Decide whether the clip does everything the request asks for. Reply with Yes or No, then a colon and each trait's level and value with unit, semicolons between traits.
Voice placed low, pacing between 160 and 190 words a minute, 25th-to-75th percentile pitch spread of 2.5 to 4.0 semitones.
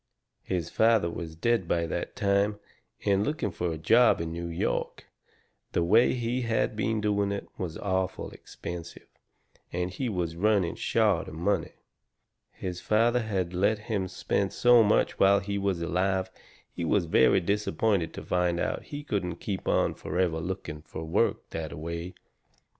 Yes: very low, 95 Hz; average, 165 wpm; average, 3.7 semitones